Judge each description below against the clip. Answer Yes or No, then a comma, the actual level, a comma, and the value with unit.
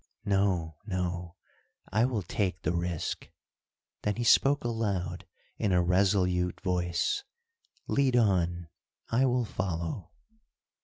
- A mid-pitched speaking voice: No, very low, 95 Hz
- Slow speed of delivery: Yes, slow, 110 wpm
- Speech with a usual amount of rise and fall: Yes, average, 3.9 semitones